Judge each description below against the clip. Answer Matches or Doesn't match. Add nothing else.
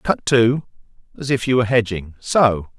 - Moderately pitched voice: Doesn't match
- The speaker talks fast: Doesn't match